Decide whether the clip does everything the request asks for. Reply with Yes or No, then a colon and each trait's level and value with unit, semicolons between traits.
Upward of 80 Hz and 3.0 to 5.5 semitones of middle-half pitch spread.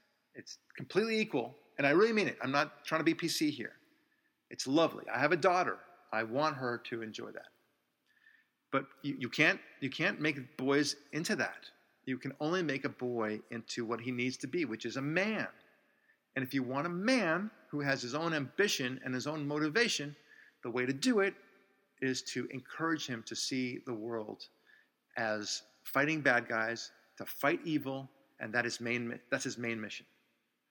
Yes: low, 135 Hz; average, 4.3 semitones